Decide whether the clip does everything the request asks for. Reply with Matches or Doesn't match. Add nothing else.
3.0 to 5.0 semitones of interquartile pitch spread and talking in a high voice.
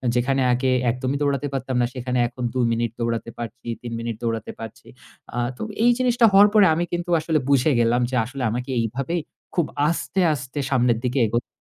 Doesn't match